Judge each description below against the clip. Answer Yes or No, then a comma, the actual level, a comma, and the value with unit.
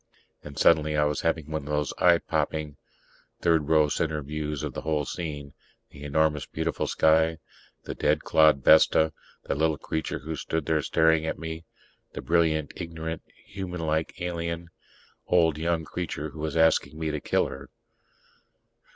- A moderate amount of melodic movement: No, narrow, 1.4 semitones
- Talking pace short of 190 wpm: Yes, average, 160 wpm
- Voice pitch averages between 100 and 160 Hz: No, very low, 80 Hz